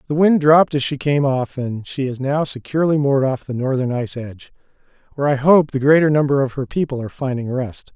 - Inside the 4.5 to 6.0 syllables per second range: No, 6.2 syllables/s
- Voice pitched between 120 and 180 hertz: Yes, low, 135 Hz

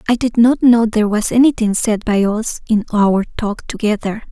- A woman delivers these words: Yes, female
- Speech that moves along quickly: No, average, 195 wpm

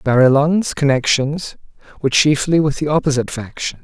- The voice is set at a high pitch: No, medium, 145 Hz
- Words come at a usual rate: No, slow, 125 wpm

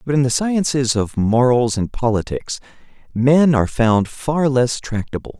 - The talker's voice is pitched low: Yes, low, 125 Hz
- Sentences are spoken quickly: No, average, 155 wpm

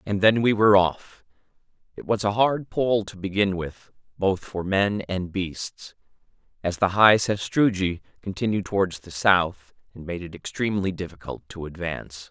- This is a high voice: No, very low, 95 Hz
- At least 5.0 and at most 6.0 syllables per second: No, 4.7 syllables/s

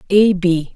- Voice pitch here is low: No, medium, 185 Hz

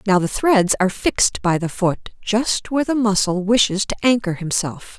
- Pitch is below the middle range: No, high, 205 Hz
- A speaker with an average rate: Yes, average, 190 wpm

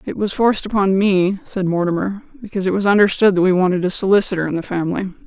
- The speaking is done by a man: No, female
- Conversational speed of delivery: No, fast, 215 wpm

